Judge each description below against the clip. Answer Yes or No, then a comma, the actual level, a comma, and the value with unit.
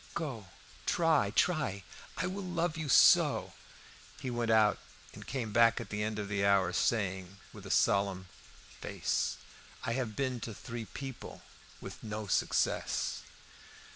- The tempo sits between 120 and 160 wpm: Yes, average, 140 wpm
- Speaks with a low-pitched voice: Yes, low, 115 Hz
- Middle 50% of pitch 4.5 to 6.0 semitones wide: Yes, average, 5.1 semitones